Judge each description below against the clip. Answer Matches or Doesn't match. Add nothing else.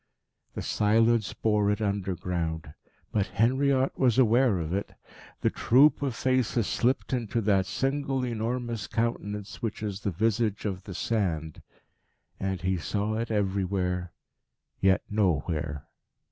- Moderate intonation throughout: Matches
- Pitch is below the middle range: Matches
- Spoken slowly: Matches